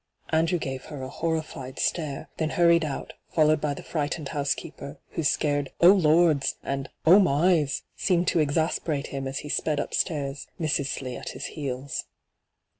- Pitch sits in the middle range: Yes, medium, 150 Hz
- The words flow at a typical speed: Yes, average, 185 wpm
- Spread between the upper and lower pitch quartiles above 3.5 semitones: No, average, 2.8 semitones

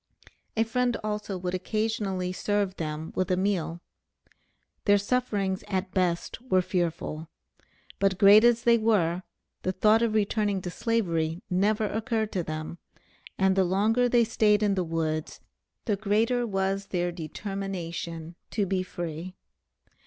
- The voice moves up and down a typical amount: Yes, average, 3.4 semitones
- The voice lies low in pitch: No, high, 195 Hz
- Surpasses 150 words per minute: No, average, 140 wpm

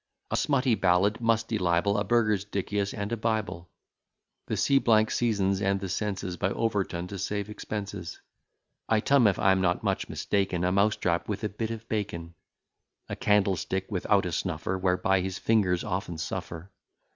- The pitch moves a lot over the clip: No, average, 2.7 semitones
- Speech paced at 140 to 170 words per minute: Yes, average, 160 wpm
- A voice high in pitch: No, low, 100 Hz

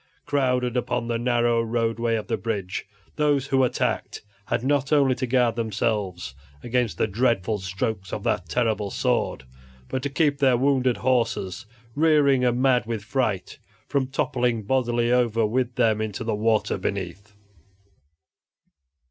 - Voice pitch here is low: Yes, low, 120 Hz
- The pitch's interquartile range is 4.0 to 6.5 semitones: No, average, 3.1 semitones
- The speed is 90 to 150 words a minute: Yes, average, 145 wpm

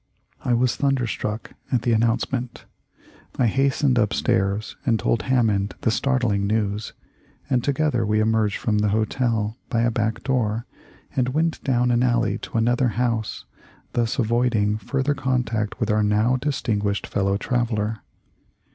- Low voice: Yes, low, 115 Hz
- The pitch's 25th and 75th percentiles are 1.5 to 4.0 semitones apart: Yes, average, 2.8 semitones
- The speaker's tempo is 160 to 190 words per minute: No, average, 145 wpm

